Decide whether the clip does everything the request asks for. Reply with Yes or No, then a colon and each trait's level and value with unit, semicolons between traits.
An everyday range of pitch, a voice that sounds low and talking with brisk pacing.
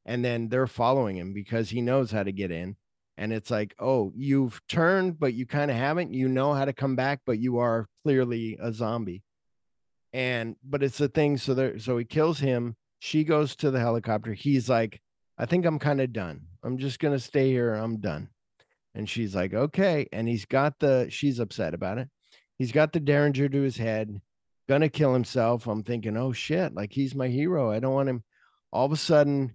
Yes: average, 3.8 semitones; low, 125 Hz; fast, 215 wpm